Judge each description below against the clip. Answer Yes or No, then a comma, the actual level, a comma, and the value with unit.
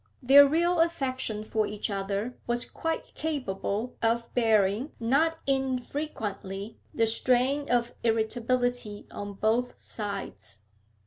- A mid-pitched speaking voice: No, high, 240 Hz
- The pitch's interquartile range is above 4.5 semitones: No, average, 4.2 semitones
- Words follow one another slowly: Yes, slow, 110 wpm